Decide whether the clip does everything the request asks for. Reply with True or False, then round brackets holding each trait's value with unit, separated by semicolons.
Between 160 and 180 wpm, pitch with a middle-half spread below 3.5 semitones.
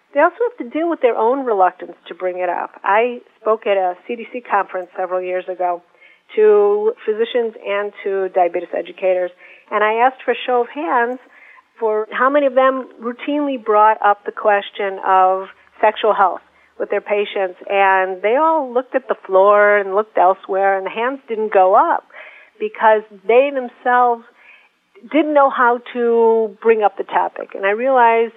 False (175 wpm; 4.8 semitones)